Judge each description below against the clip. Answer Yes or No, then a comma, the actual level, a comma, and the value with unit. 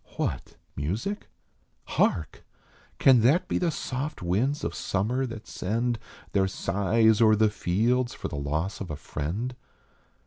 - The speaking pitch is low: Yes, low, 110 Hz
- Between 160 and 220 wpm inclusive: No, average, 145 wpm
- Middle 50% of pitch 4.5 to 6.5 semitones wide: Yes, average, 5.1 semitones